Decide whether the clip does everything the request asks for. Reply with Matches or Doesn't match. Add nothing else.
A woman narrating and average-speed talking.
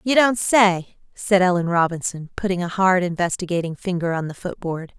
Matches